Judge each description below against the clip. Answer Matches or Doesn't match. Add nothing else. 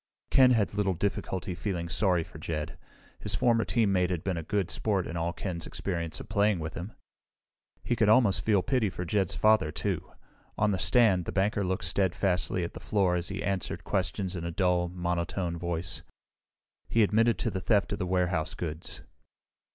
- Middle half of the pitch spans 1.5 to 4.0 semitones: Matches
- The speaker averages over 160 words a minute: Matches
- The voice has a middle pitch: Doesn't match